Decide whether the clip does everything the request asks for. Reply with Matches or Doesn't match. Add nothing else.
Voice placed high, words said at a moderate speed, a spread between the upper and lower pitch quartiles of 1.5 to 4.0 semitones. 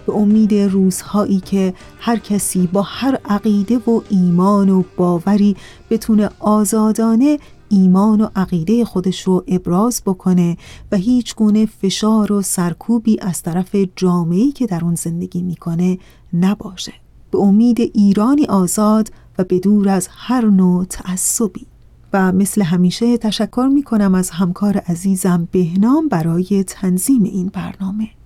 Matches